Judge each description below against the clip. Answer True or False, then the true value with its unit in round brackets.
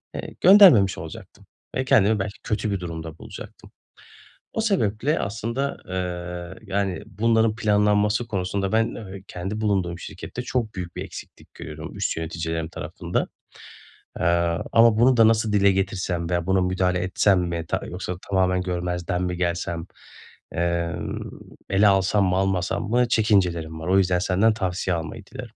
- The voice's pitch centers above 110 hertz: False (95 Hz)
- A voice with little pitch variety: False (3.3 semitones)